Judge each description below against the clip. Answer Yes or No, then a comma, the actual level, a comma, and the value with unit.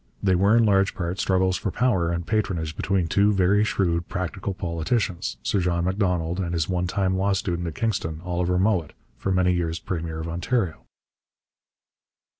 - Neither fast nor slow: Yes, average, 170 wpm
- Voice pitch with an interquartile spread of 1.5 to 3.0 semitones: Yes, narrow, 2.5 semitones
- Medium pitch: No, very low, 90 Hz